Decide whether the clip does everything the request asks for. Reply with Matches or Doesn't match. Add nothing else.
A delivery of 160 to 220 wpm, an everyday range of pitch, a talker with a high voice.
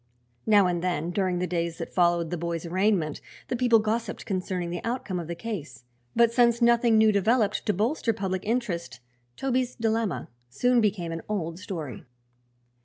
Matches